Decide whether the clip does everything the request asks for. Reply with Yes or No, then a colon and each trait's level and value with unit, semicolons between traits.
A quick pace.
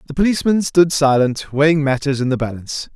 No: average, 185 wpm